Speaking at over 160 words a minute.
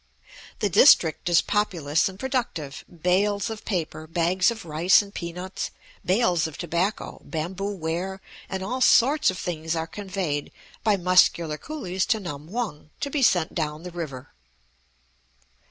No: average, 145 wpm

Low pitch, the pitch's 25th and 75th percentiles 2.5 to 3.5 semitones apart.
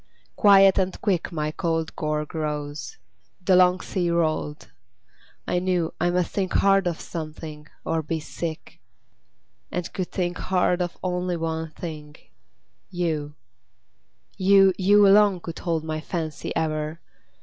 No: medium, 170 Hz; average, 2.8 semitones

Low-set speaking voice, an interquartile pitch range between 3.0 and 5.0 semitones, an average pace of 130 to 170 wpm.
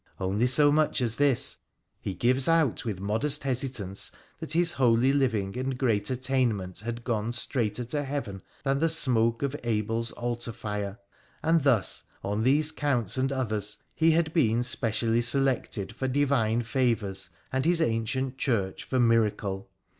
Yes: low, 120 Hz; average, 3.8 semitones; average, 155 wpm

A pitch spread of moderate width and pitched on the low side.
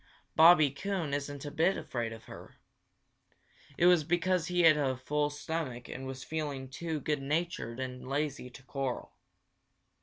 No: average, 3.6 semitones; medium, 145 Hz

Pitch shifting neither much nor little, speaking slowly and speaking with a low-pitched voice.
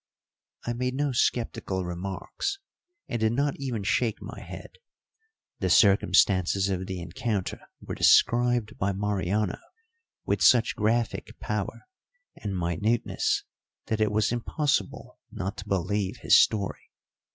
Yes: average, 3.8 semitones; slow, 125 wpm; low, 105 Hz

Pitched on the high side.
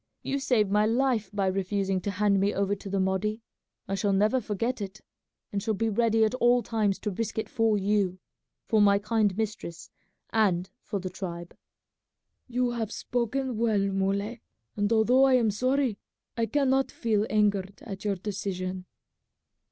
Yes: high, 210 Hz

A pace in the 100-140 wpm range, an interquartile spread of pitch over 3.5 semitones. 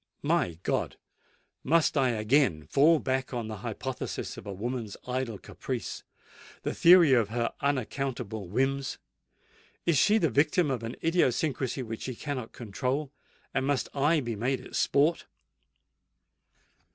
Yes: slow, 135 wpm; average, 3.9 semitones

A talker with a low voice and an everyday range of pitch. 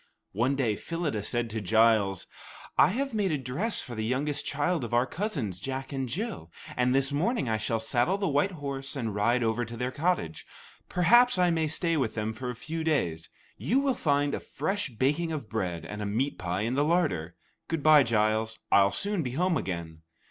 No: low, 130 Hz; wide, 6.8 semitones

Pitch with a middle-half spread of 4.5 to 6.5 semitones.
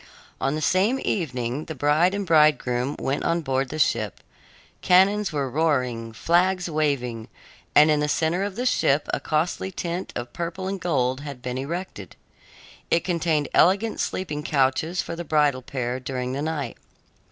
Yes: average, 4.8 semitones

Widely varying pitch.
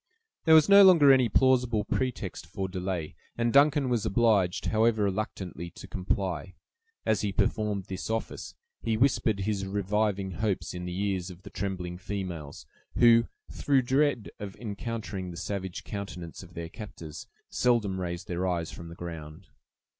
No: average, 4.3 semitones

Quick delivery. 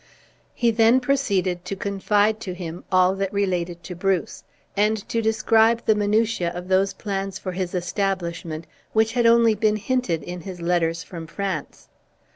No: average, 160 wpm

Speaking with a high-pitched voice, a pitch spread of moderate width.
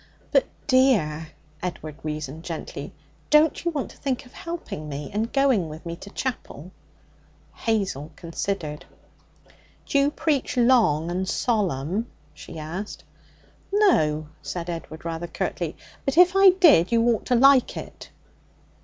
No: high, 195 Hz; wide, 8.8 semitones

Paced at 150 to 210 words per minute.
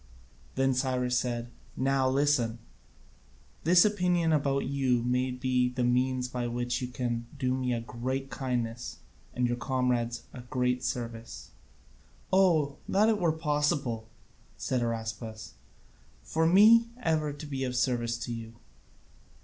No: slow, 135 wpm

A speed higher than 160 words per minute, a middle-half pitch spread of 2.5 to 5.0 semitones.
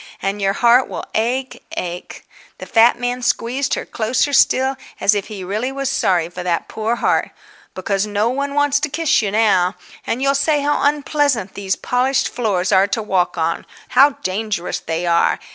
No: average, 175 wpm; wide, 5.6 semitones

